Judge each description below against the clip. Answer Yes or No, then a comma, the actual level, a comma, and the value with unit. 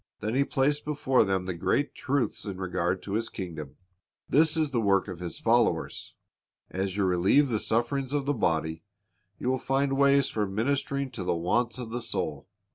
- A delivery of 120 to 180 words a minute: No, average, 190 wpm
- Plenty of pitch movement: Yes, wide, 6.7 semitones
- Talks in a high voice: No, low, 115 Hz